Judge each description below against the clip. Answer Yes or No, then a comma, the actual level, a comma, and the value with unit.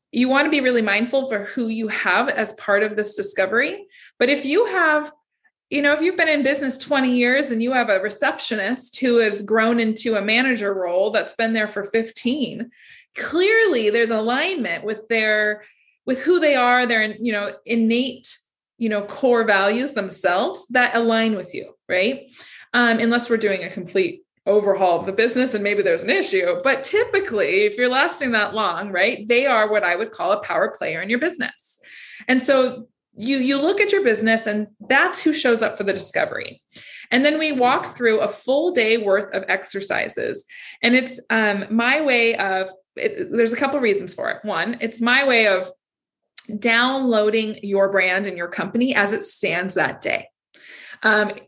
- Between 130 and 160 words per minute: No, average, 190 wpm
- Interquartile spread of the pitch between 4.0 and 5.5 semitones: Yes, average, 4.6 semitones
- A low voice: No, high, 235 Hz